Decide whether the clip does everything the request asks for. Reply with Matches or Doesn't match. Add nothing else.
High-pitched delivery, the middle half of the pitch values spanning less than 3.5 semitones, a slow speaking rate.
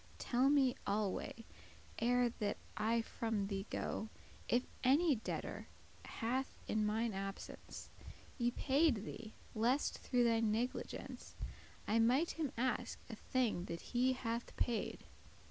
Matches